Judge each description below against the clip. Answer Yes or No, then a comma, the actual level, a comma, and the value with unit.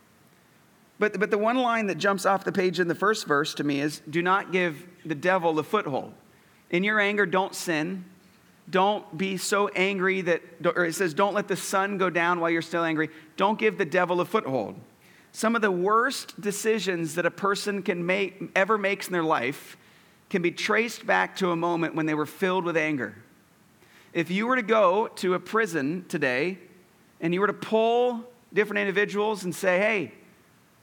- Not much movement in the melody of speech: No, average, 3.2 semitones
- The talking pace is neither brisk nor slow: Yes, average, 195 wpm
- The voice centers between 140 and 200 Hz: Yes, high, 190 Hz